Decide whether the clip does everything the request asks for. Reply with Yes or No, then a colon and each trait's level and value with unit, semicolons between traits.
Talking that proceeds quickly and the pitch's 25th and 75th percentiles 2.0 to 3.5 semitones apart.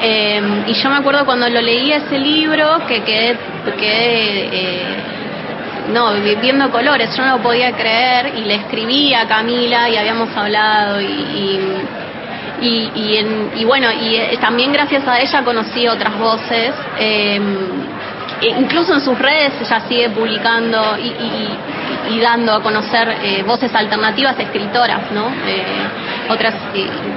No: average, 150 wpm; average, 2.7 semitones